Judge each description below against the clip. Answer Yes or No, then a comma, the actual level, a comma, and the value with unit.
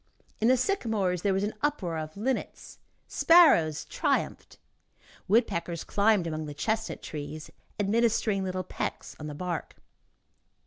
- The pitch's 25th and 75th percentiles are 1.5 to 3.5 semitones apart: No, wide, 5.4 semitones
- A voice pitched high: Yes, high, 195 Hz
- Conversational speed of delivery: No, slow, 130 wpm